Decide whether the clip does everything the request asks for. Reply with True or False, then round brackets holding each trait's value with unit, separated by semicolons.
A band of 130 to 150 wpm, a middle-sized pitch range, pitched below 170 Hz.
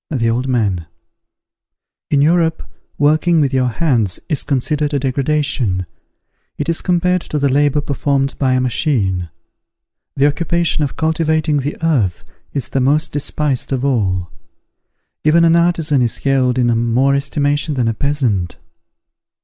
True (140 wpm; 3.4 semitones; 140 Hz)